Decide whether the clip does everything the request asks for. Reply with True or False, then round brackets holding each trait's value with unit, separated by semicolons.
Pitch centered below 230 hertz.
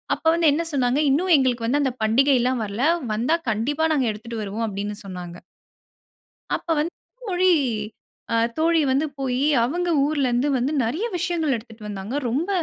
False (260 Hz)